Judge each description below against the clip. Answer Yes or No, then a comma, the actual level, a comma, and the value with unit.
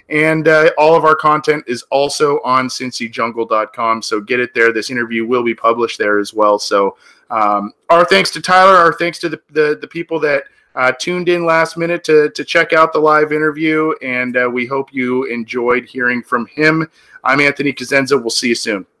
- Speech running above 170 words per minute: Yes, average, 200 wpm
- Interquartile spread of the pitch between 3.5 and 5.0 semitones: Yes, average, 4.5 semitones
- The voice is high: No, low, 135 Hz